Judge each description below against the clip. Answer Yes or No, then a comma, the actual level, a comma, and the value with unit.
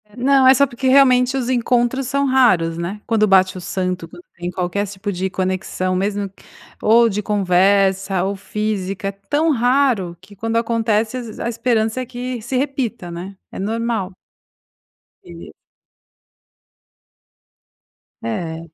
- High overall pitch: Yes, high, 210 Hz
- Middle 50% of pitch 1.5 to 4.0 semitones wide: No, average, 4.6 semitones